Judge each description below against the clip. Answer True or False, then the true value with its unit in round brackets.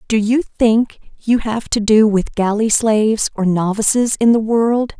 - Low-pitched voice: False (220 Hz)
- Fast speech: False (180 wpm)